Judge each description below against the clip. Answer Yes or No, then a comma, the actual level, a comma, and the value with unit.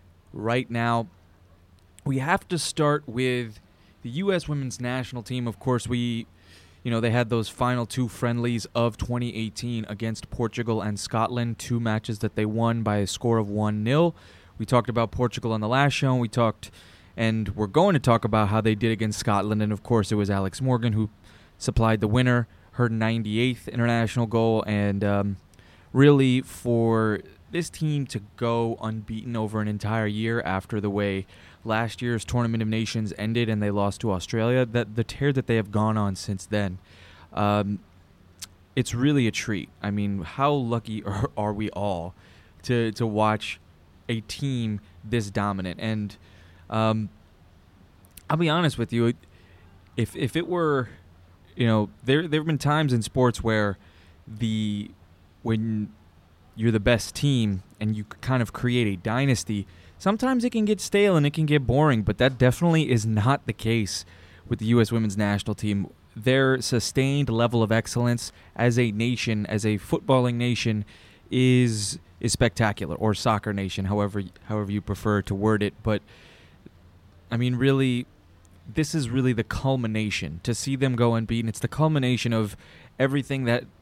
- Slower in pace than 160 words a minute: No, average, 170 wpm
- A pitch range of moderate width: Yes, average, 3.3 semitones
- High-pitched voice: No, low, 110 Hz